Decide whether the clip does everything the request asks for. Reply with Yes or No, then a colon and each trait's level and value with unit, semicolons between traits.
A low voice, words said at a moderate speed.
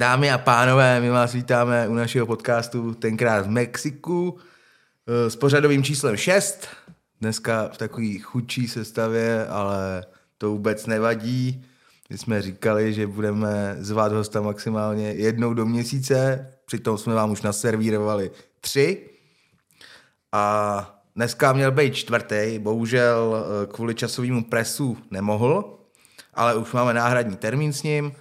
Yes: low, 115 Hz; average, 125 wpm